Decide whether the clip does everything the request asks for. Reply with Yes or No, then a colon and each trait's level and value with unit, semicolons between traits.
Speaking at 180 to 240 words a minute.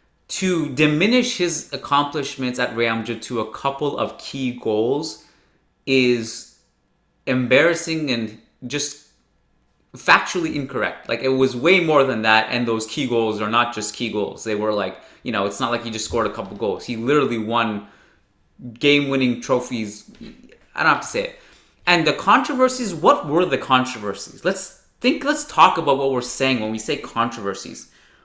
No: average, 170 wpm